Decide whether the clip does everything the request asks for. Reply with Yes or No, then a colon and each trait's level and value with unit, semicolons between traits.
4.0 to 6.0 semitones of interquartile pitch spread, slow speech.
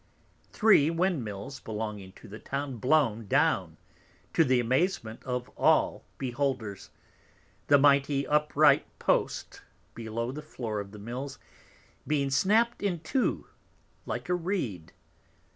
Yes: average, 5.2 semitones; slow, 120 wpm